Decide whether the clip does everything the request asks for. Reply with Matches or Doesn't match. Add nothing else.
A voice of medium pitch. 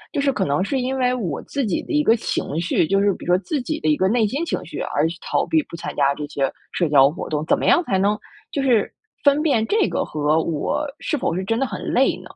Doesn't match